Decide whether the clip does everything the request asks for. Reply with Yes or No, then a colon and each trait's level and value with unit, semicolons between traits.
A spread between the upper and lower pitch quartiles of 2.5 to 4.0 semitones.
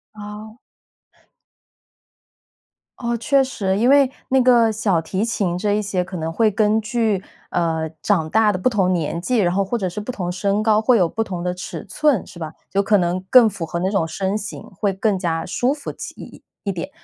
Yes: average, 3.7 semitones